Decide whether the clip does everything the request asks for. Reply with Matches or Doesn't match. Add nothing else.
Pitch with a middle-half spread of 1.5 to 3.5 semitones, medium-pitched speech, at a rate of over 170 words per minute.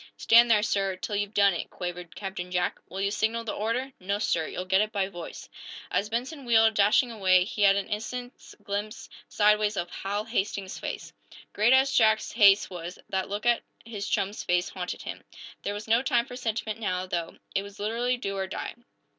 Doesn't match